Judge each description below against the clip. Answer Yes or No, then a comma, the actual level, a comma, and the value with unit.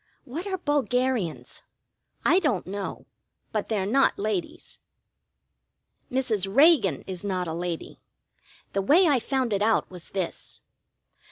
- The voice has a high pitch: Yes, high, 215 Hz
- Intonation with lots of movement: Yes, wide, 6.1 semitones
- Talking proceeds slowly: Yes, slow, 125 wpm